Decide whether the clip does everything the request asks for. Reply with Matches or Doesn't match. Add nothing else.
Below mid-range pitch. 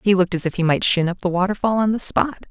Doesn't match